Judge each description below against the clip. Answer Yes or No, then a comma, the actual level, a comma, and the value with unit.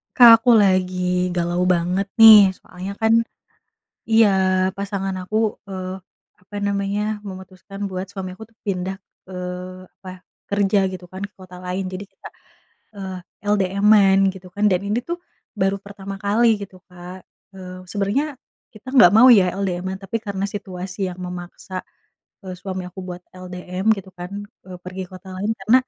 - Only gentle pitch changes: Yes, narrow, 1.8 semitones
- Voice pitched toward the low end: No, high, 190 Hz